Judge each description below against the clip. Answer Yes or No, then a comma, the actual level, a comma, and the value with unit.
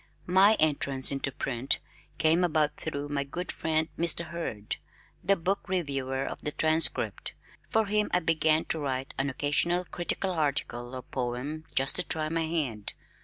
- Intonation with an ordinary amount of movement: Yes, average, 3.8 semitones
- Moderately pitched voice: Yes, medium, 155 Hz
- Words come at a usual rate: Yes, average, 160 wpm